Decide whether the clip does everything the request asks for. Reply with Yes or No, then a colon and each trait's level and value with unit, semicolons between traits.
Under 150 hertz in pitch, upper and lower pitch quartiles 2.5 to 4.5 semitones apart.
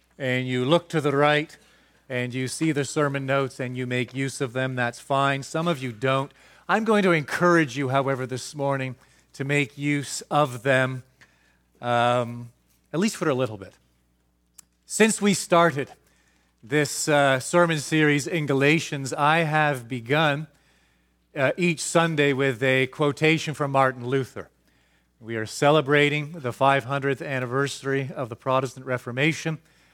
Yes: low, 135 Hz; average, 3.0 semitones